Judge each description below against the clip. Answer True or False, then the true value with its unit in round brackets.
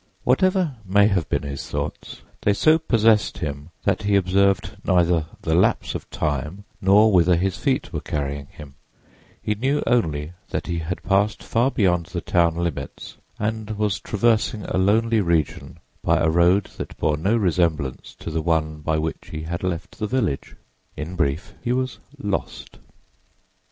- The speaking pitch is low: True (90 Hz)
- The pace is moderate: True (165 wpm)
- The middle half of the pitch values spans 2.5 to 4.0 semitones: False (4.8 semitones)